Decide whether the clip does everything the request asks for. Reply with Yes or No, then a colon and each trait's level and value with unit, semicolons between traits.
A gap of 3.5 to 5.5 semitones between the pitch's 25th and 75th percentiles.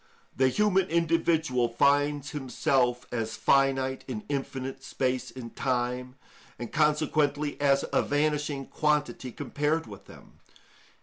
No: average, 2.8 semitones